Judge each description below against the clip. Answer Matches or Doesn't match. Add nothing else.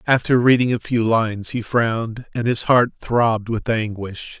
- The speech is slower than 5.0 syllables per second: Matches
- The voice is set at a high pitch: Doesn't match